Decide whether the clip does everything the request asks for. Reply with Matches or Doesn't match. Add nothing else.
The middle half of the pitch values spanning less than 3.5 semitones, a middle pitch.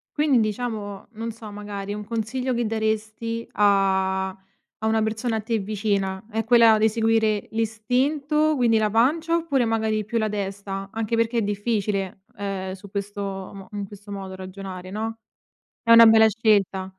Doesn't match